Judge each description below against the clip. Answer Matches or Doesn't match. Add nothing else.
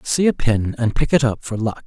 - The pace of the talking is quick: Matches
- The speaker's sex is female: Doesn't match